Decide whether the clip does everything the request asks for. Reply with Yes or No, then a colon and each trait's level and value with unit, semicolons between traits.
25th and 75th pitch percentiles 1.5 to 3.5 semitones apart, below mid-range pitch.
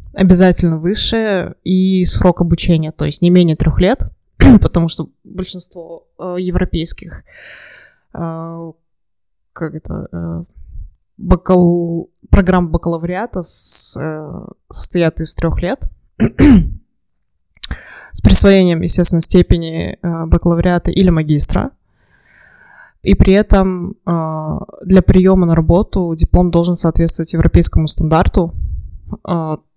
No: narrow, 2.4 semitones; medium, 170 Hz